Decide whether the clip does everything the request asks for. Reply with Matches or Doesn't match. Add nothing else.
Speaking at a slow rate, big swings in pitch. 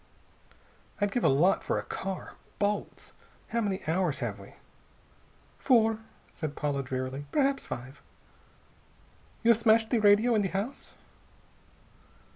Matches